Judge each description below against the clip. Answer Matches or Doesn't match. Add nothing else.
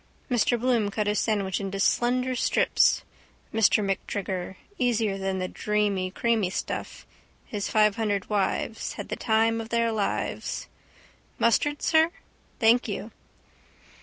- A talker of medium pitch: Doesn't match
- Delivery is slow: Matches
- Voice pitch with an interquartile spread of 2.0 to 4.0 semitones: Matches